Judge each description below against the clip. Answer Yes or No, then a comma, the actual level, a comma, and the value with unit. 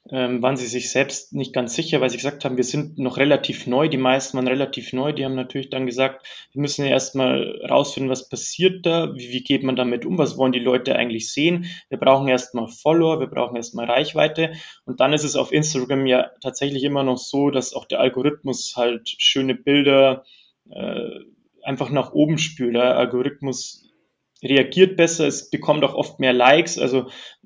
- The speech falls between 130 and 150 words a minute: No, fast, 190 wpm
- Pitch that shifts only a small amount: Yes, narrow, 2.1 semitones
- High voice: No, low, 135 Hz